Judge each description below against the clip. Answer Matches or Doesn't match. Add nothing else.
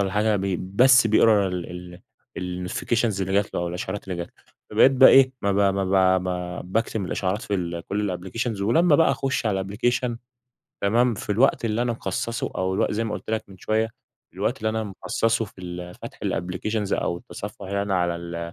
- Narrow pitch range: Doesn't match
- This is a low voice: Matches